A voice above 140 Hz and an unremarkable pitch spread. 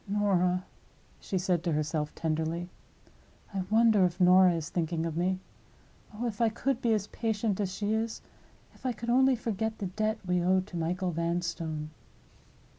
Yes: medium, 185 Hz; average, 4.2 semitones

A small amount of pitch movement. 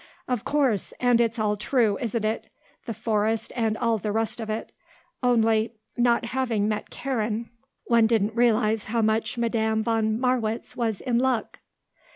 Yes: narrow, 1.6 semitones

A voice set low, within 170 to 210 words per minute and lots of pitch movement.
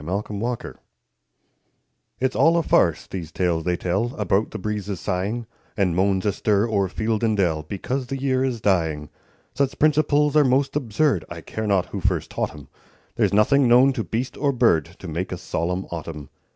Yes: low, 105 Hz; average, 180 wpm; wide, 6.1 semitones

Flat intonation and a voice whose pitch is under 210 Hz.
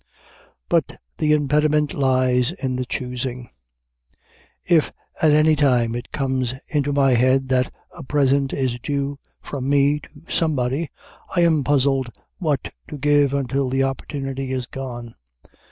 Yes: narrow, 2.2 semitones; low, 135 Hz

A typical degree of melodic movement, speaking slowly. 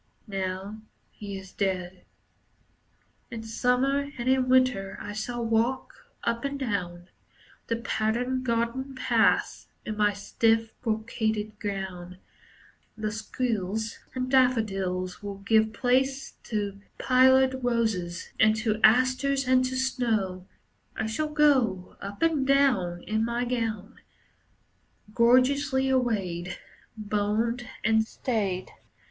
Yes: average, 4.0 semitones; slow, 110 wpm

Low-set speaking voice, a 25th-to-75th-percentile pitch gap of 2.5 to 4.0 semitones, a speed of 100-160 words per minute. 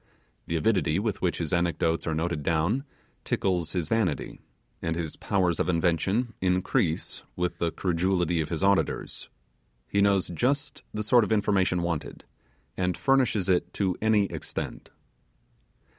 Yes: very low, 90 Hz; average, 3.2 semitones; slow, 135 wpm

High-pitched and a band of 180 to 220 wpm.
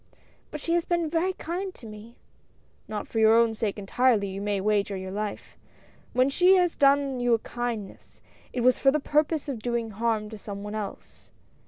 Yes: high, 235 Hz; average, 195 wpm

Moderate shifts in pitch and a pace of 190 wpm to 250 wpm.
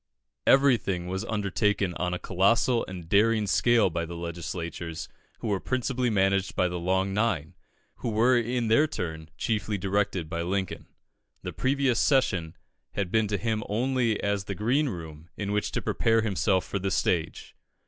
No: average, 4.3 semitones; average, 165 wpm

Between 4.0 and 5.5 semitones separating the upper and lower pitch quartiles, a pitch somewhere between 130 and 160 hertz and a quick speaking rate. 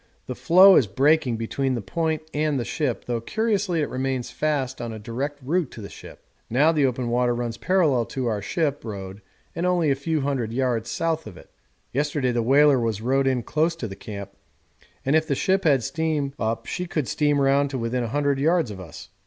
Yes: average, 4.6 semitones; low, 135 Hz; fast, 220 wpm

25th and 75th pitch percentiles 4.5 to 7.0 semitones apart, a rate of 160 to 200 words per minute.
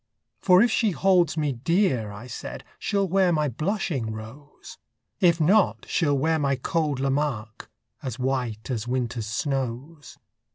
No: wide, 5.5 semitones; average, 140 wpm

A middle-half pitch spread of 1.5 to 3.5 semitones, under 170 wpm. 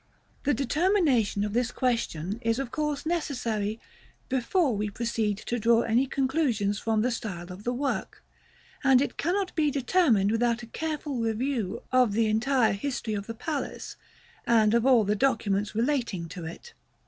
No: average, 4.3 semitones; average, 160 wpm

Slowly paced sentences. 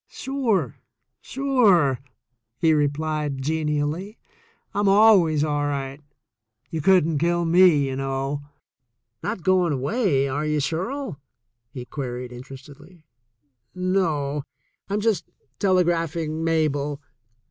Yes: slow, 105 wpm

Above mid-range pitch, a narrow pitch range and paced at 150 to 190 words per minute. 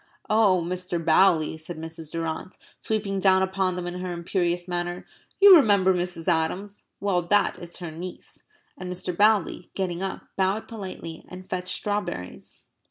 No: medium, 180 Hz; narrow, 2.1 semitones; average, 155 wpm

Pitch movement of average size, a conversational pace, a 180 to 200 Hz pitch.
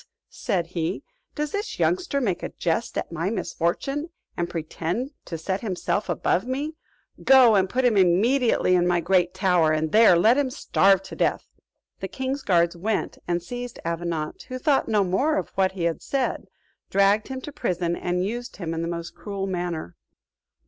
No: wide, 6.2 semitones; average, 180 wpm; high, 190 Hz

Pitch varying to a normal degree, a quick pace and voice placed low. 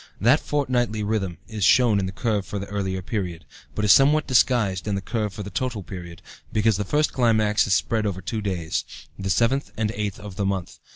Yes: average, 3.0 semitones; fast, 215 wpm; low, 105 Hz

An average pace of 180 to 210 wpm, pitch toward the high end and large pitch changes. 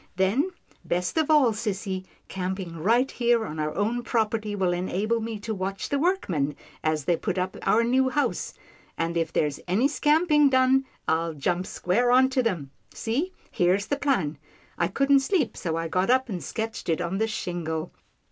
Yes: average, 185 wpm; high, 205 Hz; wide, 6.5 semitones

